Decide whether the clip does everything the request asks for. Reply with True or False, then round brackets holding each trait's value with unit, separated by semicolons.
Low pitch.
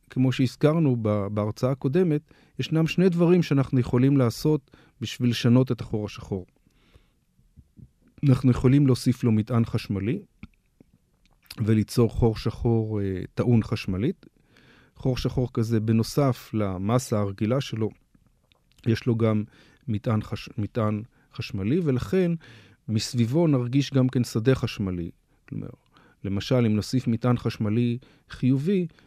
True (120 Hz)